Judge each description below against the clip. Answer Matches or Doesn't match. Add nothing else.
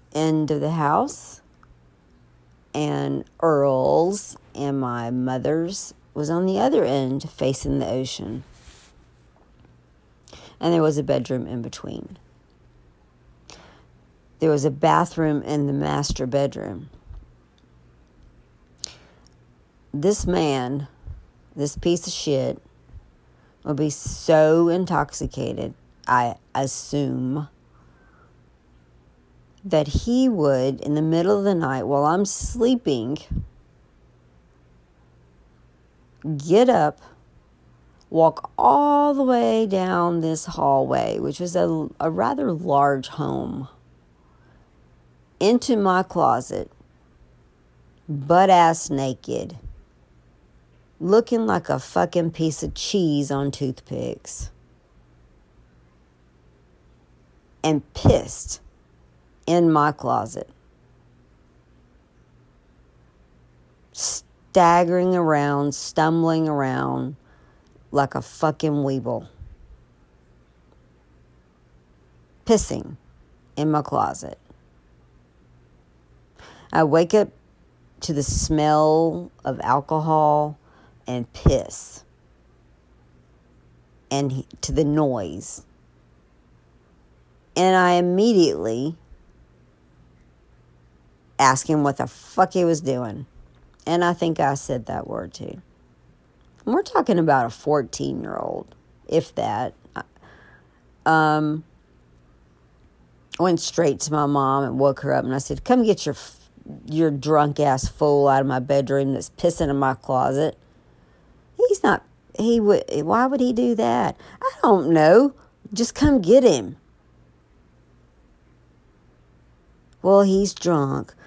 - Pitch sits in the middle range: Doesn't match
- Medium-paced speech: Doesn't match